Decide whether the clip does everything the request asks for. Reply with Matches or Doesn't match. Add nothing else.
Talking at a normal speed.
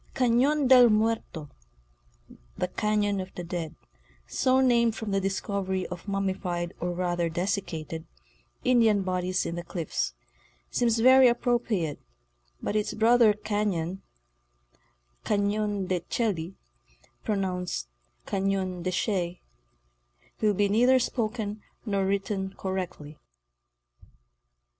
Doesn't match